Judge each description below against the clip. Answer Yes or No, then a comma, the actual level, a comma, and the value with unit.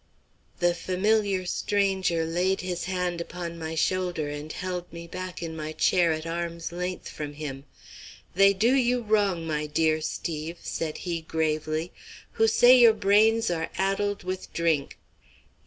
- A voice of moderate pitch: Yes, medium, 175 Hz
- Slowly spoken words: No, average, 150 wpm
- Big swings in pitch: No, average, 3.2 semitones